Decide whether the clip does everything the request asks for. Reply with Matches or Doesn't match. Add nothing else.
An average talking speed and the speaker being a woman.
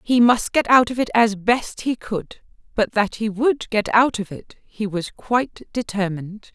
Matches